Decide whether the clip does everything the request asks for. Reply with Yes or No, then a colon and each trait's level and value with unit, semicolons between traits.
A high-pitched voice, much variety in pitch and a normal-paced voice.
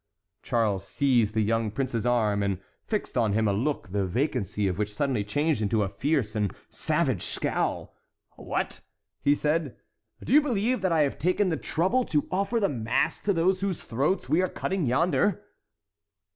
No: low, 135 Hz; wide, 8.9 semitones; average, 175 wpm